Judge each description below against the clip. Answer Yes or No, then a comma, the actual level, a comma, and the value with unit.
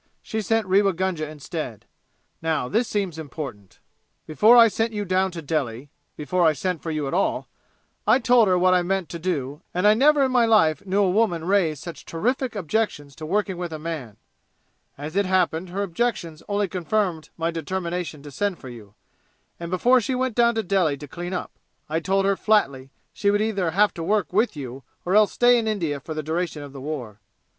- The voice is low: No, medium, 180 Hz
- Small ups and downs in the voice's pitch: No, average, 5.0 semitones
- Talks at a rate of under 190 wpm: No, fast, 205 wpm